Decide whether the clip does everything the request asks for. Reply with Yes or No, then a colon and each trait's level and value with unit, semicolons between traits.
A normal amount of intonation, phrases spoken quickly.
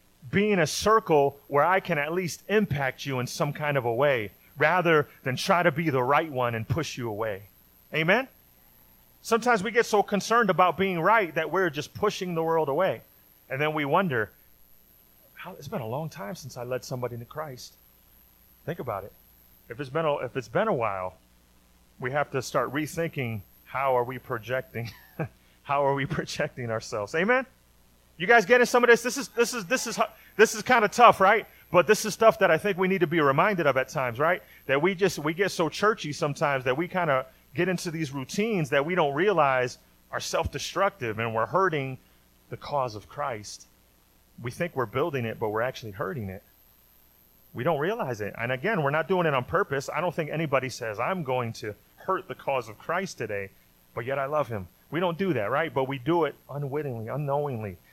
No: wide, 7.0 semitones; fast, 210 wpm